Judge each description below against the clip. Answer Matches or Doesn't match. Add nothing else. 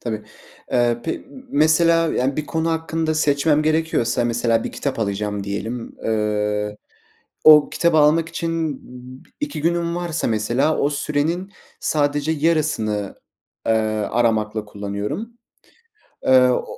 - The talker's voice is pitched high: Doesn't match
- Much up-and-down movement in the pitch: Matches